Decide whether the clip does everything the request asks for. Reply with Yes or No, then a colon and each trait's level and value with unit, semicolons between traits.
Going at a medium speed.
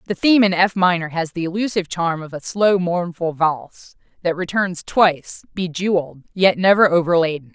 Yes: average, 165 wpm